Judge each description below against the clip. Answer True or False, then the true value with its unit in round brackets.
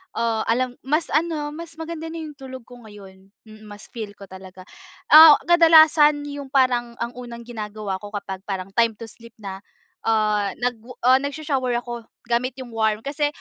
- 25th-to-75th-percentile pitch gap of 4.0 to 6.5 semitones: True (5.4 semitones)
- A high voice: True (240 Hz)